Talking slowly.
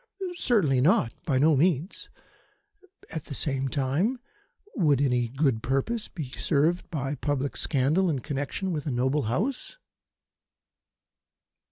Yes: slow, 125 wpm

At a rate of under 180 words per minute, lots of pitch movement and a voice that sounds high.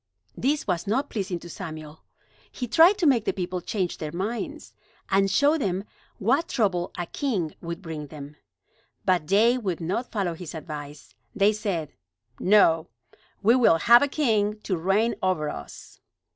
Yes: average, 160 wpm; wide, 5.7 semitones; high, 195 Hz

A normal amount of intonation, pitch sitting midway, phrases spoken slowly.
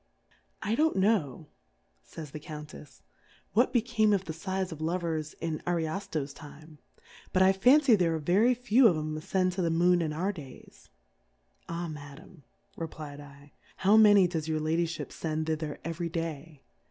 No: average, 3.7 semitones; medium, 165 Hz; average, 165 wpm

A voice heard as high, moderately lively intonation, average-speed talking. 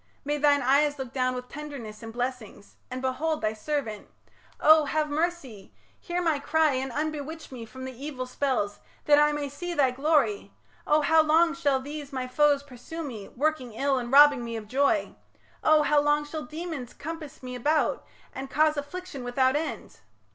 Yes: very high, 285 Hz; average, 3.2 semitones; average, 180 wpm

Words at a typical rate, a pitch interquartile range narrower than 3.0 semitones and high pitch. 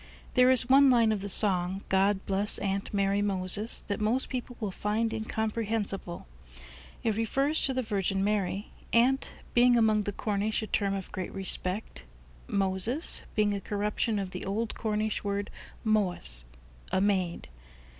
Yes: average, 155 wpm; narrow, 2.5 semitones; high, 205 Hz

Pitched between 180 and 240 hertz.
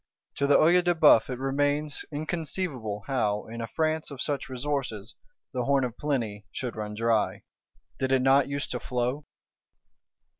No: low, 135 Hz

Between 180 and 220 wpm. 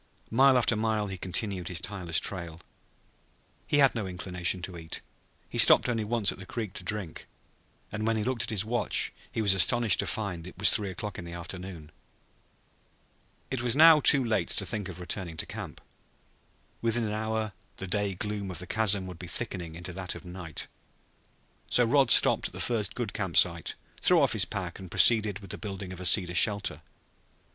Yes: average, 200 wpm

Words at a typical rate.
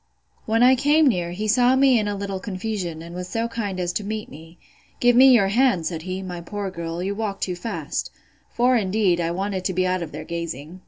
No: fast, 230 wpm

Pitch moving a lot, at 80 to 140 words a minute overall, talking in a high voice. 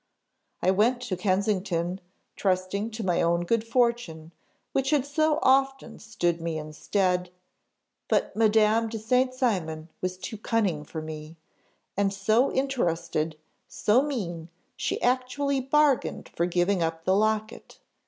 Yes: wide, 6.1 semitones; slow, 135 wpm; high, 205 Hz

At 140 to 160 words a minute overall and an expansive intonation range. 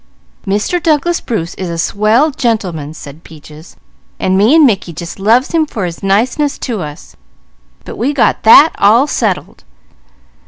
Yes: average, 155 wpm; wide, 8.2 semitones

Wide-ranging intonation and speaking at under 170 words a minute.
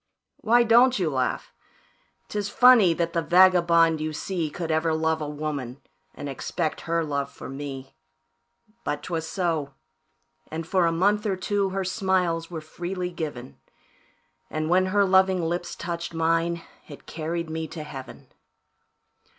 No: average, 3.1 semitones; average, 150 wpm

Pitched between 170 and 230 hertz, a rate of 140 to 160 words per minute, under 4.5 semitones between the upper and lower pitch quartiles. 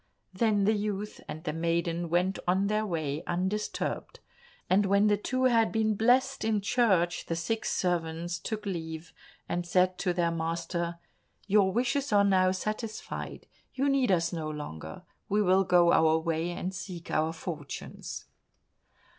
Yes: medium, 185 Hz; average, 155 wpm; average, 4.0 semitones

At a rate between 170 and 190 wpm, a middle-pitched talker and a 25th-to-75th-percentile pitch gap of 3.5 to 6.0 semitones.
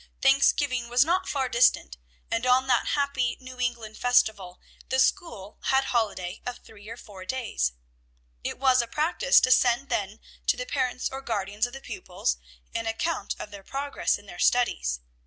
No: average, 175 wpm; high, 245 Hz; average, 4.3 semitones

